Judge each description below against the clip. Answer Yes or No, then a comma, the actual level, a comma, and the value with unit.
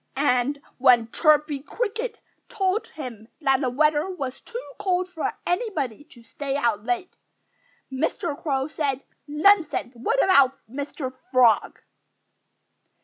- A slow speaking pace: Yes, slow, 120 wpm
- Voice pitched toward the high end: Yes, very high, 290 Hz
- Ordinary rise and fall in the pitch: No, wide, 5.8 semitones